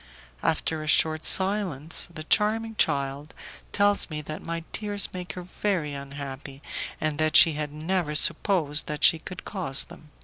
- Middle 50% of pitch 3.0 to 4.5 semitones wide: Yes, average, 4.1 semitones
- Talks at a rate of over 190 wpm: No, average, 160 wpm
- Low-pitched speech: No, medium, 155 Hz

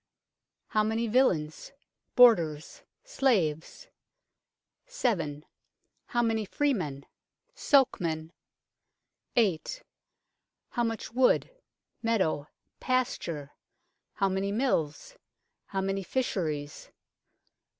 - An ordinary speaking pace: No, slow, 75 wpm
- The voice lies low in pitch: No, high, 200 Hz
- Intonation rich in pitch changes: Yes, wide, 7.5 semitones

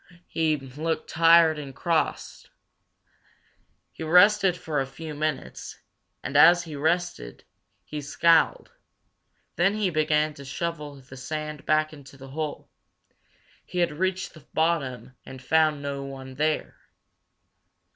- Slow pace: Yes, slow, 125 wpm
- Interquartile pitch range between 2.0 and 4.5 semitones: Yes, average, 2.9 semitones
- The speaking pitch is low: No, medium, 155 Hz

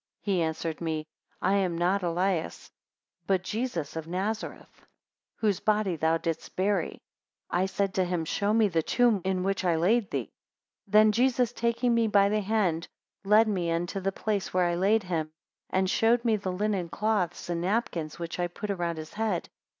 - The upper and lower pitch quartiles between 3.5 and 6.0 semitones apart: Yes, average, 3.8 semitones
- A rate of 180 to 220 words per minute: Yes, average, 185 wpm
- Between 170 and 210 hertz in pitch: Yes, high, 190 Hz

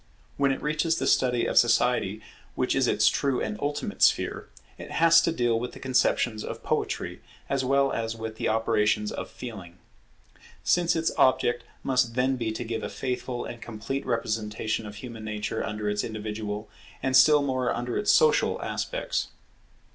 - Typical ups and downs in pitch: Yes, average, 3.7 semitones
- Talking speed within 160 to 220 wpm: Yes, average, 170 wpm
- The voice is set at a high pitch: No, low, 120 Hz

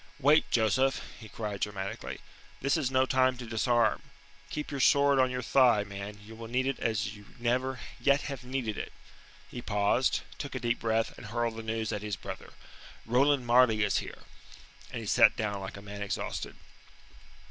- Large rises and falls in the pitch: No, average, 3.5 semitones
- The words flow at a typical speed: Yes, average, 185 wpm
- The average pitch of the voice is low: Yes, low, 120 Hz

